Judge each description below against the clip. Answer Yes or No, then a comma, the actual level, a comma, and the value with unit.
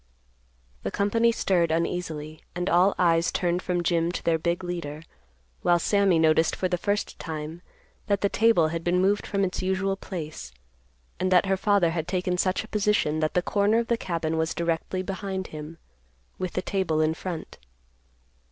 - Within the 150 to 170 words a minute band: No, average, 180 wpm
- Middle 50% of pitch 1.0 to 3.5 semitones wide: Yes, average, 2.9 semitones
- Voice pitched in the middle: Yes, medium, 180 Hz